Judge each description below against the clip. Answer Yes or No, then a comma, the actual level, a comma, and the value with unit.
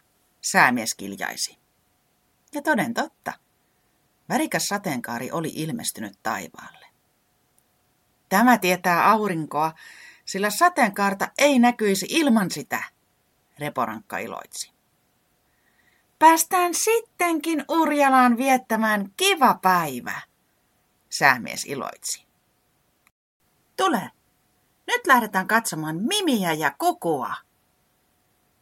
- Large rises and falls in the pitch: Yes, wide, 8.6 semitones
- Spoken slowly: Yes, slow, 75 wpm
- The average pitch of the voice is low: No, high, 240 Hz